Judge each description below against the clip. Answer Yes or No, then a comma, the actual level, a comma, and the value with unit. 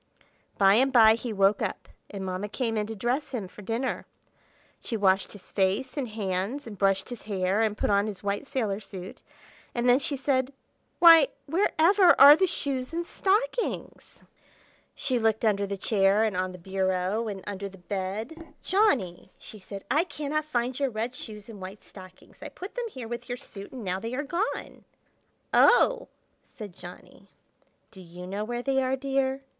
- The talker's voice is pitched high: Yes, high, 225 Hz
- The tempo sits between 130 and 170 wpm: No, average, 185 wpm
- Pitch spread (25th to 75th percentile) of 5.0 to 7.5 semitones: Yes, wide, 5.4 semitones